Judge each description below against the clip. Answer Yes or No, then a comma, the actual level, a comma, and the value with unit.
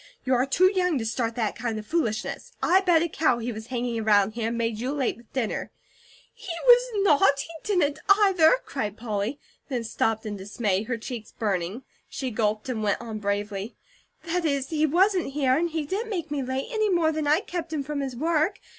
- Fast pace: Yes, fast, 210 wpm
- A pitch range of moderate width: No, wide, 6.7 semitones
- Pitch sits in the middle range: No, very high, 265 Hz